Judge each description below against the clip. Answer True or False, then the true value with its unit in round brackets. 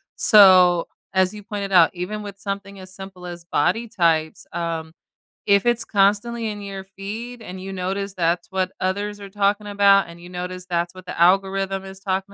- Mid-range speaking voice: False (195 Hz)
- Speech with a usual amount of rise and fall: False (2.0 semitones)